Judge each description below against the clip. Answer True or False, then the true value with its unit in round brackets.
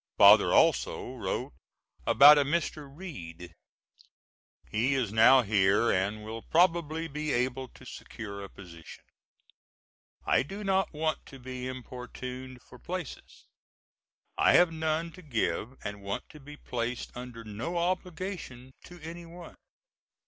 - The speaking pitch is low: True (130 Hz)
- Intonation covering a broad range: True (6.3 semitones)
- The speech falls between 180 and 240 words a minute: False (135 wpm)